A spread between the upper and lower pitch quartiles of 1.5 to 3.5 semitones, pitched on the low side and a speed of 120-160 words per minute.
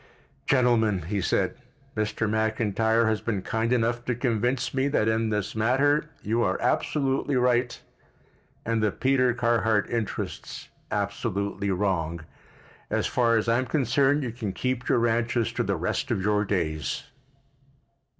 Yes: average, 3.0 semitones; low, 115 Hz; average, 145 wpm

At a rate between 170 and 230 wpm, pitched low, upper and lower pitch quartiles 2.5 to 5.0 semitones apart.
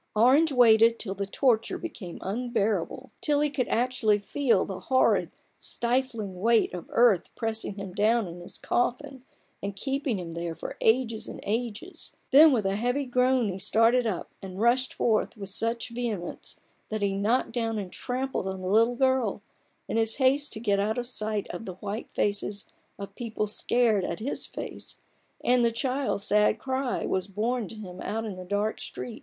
No: average, 180 wpm; high, 225 Hz; average, 3.7 semitones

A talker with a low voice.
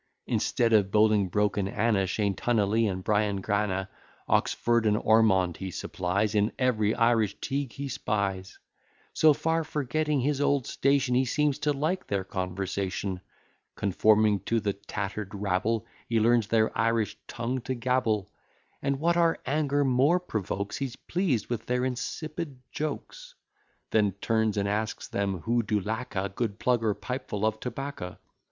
Yes: low, 110 Hz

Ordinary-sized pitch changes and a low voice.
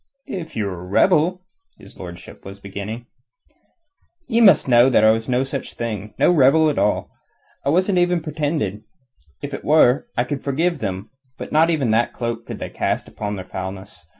No: wide, 7.4 semitones; low, 130 Hz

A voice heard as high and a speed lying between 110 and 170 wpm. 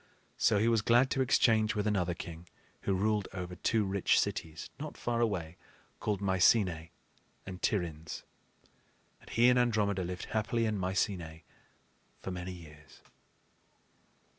No: low, 100 Hz; average, 140 wpm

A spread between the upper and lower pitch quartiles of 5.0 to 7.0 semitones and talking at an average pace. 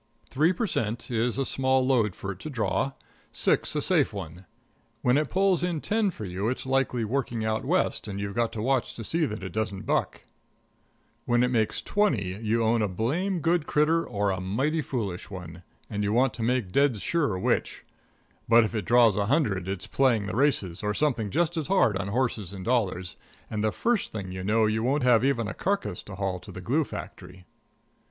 No: average, 5.3 semitones; fast, 210 wpm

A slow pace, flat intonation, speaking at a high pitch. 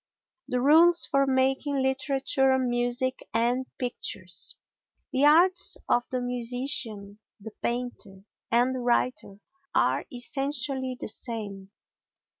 Yes: slow, 105 wpm; narrow, 2.2 semitones; very high, 250 Hz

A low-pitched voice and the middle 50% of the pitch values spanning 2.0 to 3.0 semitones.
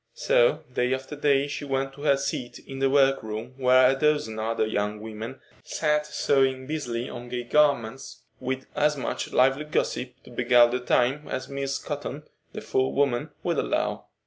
Yes: low, 130 Hz; narrow, 2.5 semitones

